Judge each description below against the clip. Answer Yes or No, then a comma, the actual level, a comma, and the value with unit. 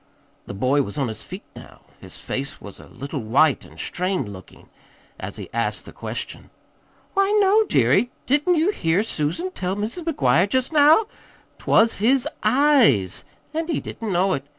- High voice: Yes, high, 195 Hz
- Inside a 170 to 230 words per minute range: Yes, average, 175 wpm